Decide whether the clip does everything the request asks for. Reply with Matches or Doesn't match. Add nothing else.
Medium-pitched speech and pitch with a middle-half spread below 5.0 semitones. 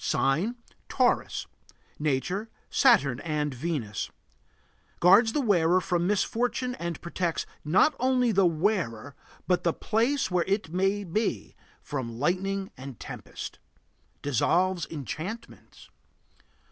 Doesn't match